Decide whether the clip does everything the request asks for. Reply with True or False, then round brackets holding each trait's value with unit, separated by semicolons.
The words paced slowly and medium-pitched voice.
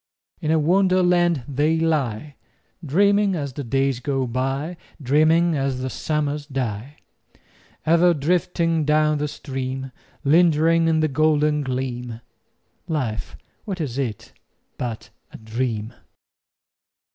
True (115 wpm; 145 Hz)